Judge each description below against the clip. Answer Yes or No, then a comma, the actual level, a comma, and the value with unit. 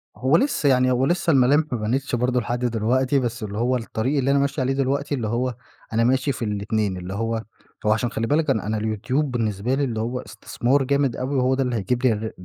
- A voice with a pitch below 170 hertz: Yes, low, 125 Hz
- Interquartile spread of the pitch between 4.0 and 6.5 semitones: No, average, 3.2 semitones